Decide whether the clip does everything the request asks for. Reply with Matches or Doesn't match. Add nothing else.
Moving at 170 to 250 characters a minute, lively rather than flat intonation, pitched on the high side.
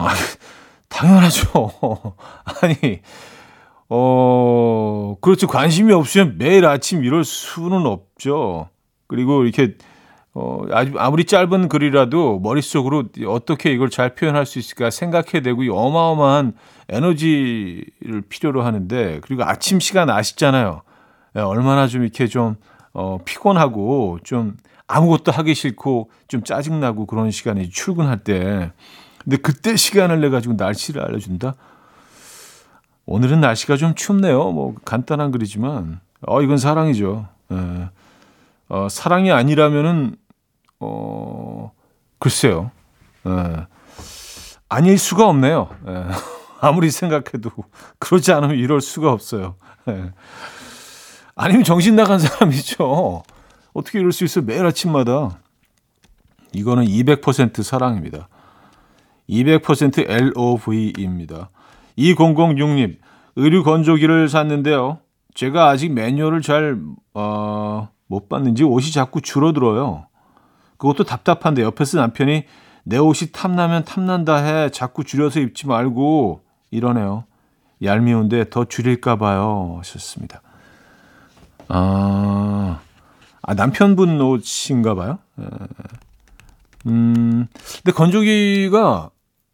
Doesn't match